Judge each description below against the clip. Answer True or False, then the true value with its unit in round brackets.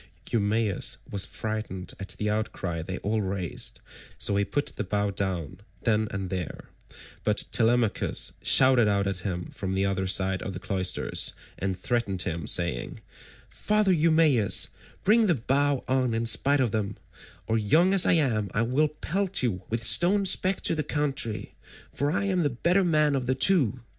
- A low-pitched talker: True (110 Hz)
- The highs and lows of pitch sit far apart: True (6.9 semitones)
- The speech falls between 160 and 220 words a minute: True (175 wpm)